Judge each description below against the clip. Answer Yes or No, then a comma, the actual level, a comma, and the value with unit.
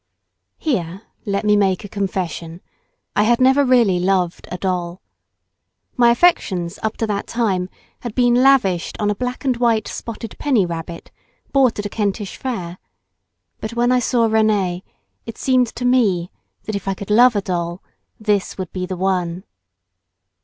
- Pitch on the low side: No, high, 205 Hz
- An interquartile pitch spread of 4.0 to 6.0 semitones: Yes, average, 4.6 semitones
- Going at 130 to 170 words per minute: Yes, average, 165 wpm